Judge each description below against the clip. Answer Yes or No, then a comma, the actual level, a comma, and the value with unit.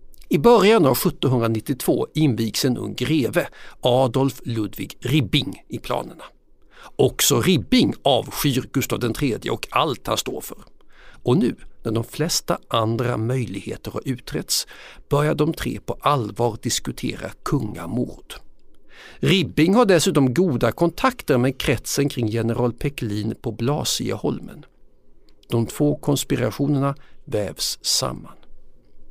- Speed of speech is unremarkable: No, slow, 115 wpm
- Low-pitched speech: Yes, low, 125 Hz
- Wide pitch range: No, average, 4.1 semitones